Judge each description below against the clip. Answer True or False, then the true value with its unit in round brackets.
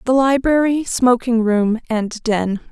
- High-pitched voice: True (240 Hz)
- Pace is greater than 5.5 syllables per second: False (3.7 syllables/s)